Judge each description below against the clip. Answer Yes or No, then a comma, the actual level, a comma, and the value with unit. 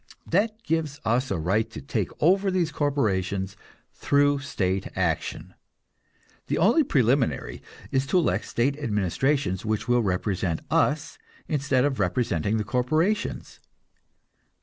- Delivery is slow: Yes, slow, 125 wpm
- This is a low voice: Yes, low, 130 Hz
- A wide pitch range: Yes, wide, 6.3 semitones